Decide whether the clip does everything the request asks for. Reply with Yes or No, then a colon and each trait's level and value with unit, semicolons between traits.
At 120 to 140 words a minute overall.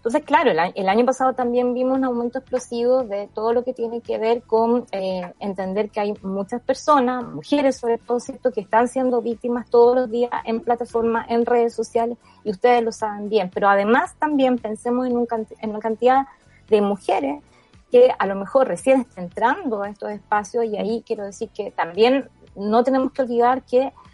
No: fast, 190 wpm